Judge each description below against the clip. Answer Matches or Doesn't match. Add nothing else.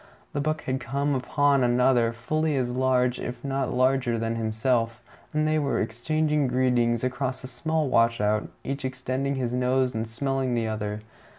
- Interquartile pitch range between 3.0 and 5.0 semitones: Doesn't match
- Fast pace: Doesn't match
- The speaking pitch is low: Matches